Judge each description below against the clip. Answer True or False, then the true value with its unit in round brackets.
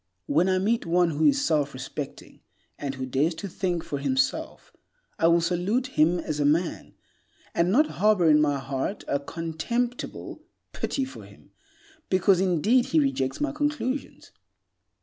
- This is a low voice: False (170 Hz)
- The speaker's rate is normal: True (155 wpm)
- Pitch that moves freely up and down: True (7.4 semitones)